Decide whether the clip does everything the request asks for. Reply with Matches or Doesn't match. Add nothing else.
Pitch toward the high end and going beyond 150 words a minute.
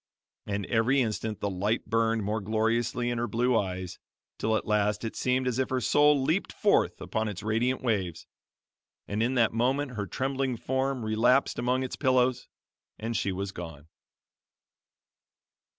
Doesn't match